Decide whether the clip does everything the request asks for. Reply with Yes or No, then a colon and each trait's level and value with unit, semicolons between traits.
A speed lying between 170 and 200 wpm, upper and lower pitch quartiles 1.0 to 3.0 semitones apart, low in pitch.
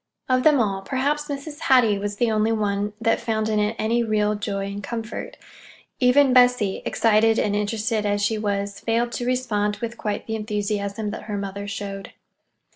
No: average, 180 wpm; narrow, 2.6 semitones; high, 215 Hz